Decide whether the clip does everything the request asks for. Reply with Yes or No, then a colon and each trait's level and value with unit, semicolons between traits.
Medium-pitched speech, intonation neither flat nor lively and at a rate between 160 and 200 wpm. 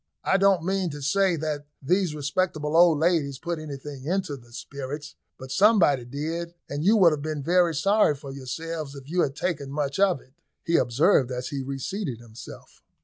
Yes: medium, 150 Hz; average, 4.2 semitones; average, 185 wpm